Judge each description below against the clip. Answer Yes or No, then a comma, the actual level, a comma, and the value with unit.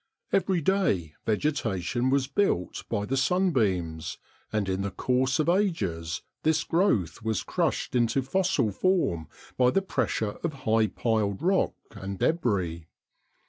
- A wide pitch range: Yes, wide, 8.9 semitones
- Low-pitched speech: Yes, low, 120 Hz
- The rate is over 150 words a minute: No, slow, 135 wpm